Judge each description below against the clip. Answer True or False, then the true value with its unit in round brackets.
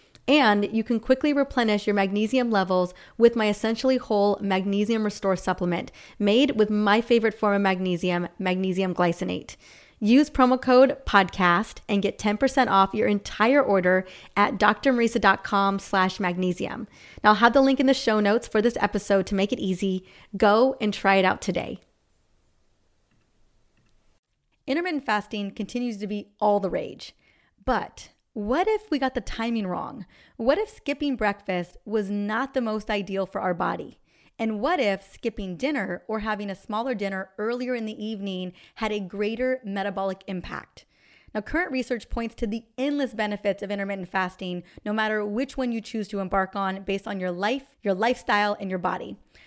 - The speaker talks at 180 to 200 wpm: False (165 wpm)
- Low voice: False (210 Hz)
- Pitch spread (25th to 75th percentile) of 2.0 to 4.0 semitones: True (3.5 semitones)